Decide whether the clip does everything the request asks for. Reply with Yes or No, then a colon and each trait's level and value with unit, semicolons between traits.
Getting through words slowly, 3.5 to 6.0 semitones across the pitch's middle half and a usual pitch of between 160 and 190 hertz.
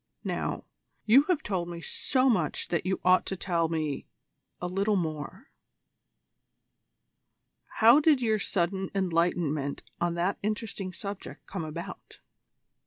Yes: slow, 125 wpm; average, 3.8 semitones; medium, 185 Hz